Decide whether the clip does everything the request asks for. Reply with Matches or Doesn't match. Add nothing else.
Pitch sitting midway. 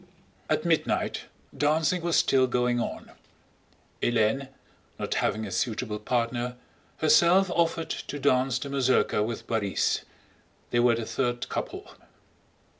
Doesn't match